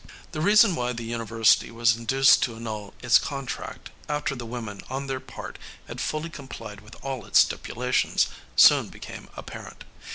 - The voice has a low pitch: Yes, low, 120 Hz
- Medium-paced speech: Yes, average, 160 wpm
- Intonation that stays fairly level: No, average, 3.3 semitones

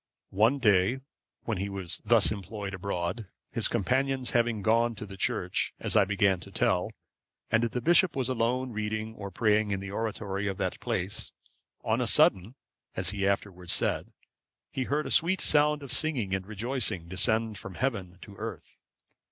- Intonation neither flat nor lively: Yes, average, 3.8 semitones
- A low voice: Yes, low, 110 Hz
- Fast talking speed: No, average, 170 wpm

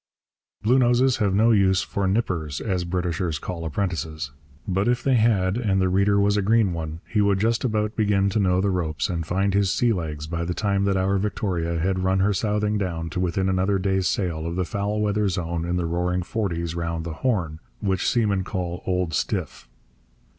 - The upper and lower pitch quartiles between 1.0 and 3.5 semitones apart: Yes, average, 3.2 semitones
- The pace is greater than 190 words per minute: Yes, average, 200 wpm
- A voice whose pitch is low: Yes, very low, 95 Hz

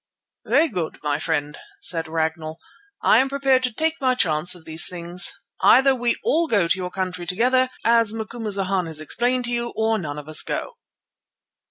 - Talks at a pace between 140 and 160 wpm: No, average, 180 wpm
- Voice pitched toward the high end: Yes, high, 195 Hz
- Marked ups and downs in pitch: Yes, wide, 7.1 semitones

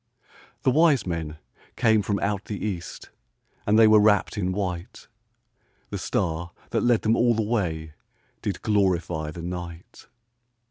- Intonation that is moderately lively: Yes, average, 4.0 semitones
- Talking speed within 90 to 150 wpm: Yes, average, 145 wpm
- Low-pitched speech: Yes, low, 100 Hz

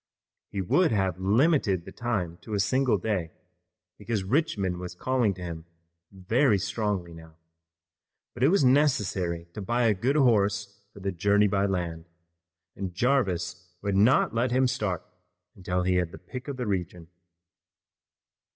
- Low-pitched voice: Yes, low, 100 Hz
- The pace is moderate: Yes, average, 155 wpm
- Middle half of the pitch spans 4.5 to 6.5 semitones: Yes, average, 5.1 semitones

